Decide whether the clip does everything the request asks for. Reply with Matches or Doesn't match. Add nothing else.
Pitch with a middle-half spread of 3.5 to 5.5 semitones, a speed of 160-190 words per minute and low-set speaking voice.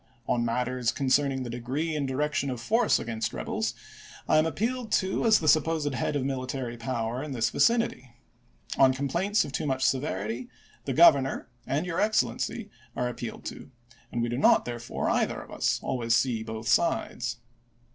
Matches